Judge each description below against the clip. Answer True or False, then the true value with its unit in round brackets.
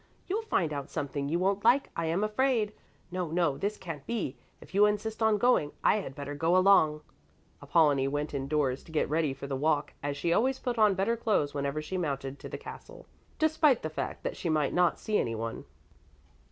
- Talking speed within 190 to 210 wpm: True (205 wpm)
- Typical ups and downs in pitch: False (6.6 semitones)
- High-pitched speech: False (165 Hz)